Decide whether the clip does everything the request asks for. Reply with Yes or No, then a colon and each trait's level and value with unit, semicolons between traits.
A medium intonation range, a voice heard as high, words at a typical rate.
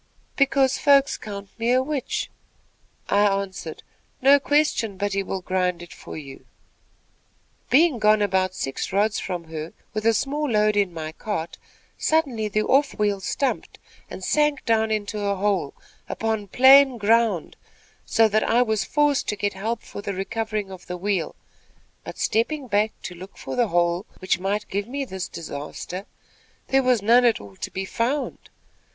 Yes: average, 4.6 semitones; high, 210 Hz; average, 165 wpm